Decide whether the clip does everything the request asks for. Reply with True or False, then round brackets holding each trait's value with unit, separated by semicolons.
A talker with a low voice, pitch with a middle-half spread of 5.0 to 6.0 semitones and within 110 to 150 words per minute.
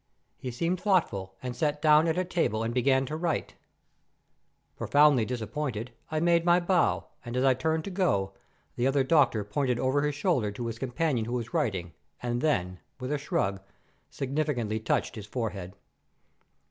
False (130 Hz; 5.4 semitones; 170 wpm)